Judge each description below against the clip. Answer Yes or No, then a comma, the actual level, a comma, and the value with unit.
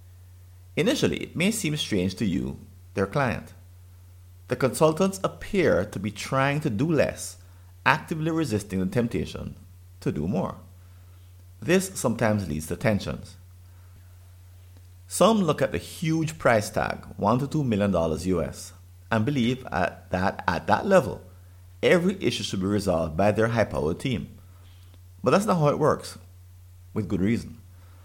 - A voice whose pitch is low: Yes, very low, 95 Hz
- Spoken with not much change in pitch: No, average, 4.1 semitones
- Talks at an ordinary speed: Yes, average, 145 wpm